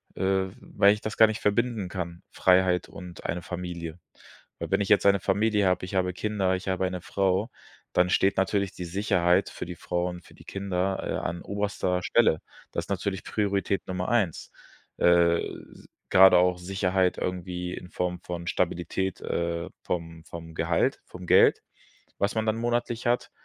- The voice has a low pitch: Yes, very low, 90 Hz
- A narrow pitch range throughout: Yes, narrow, 2.1 semitones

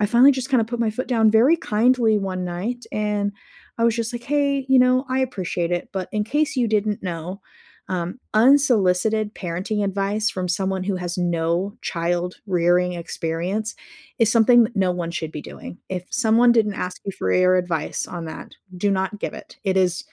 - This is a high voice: Yes, high, 205 Hz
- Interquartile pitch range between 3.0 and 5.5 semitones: Yes, average, 4.5 semitones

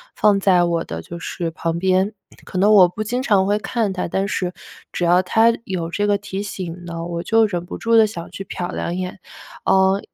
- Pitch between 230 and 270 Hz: No, high, 190 Hz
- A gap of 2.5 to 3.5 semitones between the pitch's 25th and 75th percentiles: Yes, average, 2.9 semitones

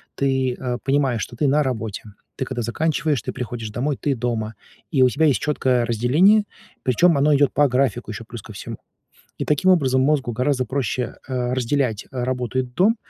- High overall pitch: No, low, 130 Hz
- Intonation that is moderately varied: Yes, average, 3.0 semitones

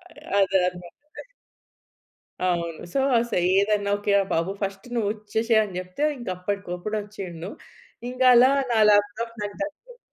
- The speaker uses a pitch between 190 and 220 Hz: Yes, high, 205 Hz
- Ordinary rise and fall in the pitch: Yes, average, 3.8 semitones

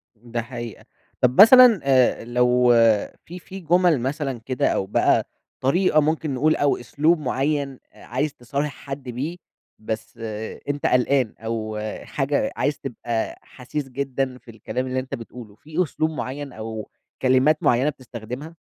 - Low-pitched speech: Yes, low, 130 Hz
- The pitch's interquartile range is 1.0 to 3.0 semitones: No, average, 3.7 semitones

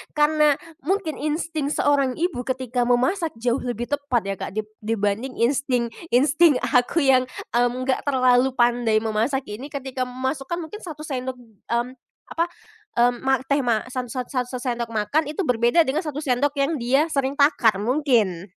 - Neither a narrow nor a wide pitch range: Yes, average, 3.3 semitones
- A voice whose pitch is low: No, very high, 260 Hz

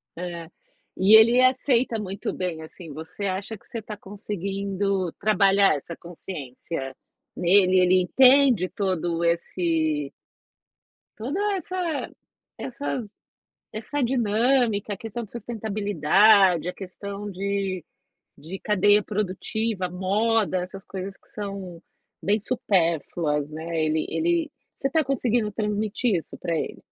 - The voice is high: Yes, high, 200 Hz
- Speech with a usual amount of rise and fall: Yes, average, 3.7 semitones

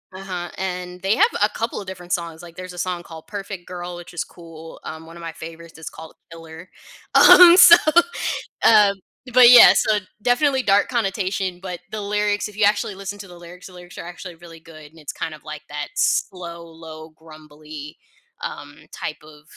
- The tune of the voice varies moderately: Yes, average, 3.5 semitones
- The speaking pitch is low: No, medium, 175 Hz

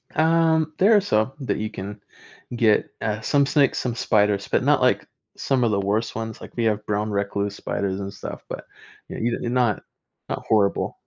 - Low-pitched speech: Yes, low, 110 Hz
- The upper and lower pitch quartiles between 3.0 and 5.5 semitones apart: Yes, average, 4.1 semitones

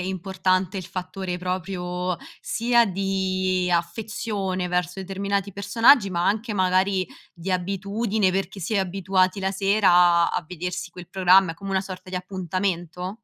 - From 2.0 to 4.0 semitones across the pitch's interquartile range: No, narrow, 1.5 semitones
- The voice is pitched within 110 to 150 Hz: No, medium, 185 Hz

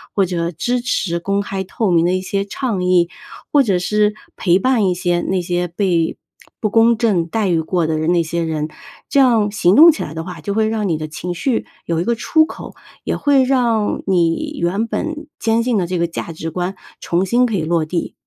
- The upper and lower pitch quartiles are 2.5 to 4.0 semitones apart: No, average, 4.8 semitones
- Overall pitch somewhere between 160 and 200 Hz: Yes, high, 190 Hz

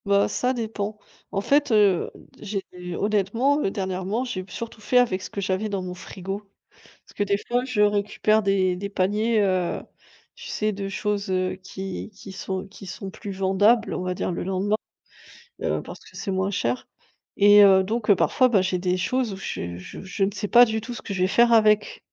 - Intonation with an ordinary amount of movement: No, narrow, 2.3 semitones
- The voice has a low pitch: No, high, 200 Hz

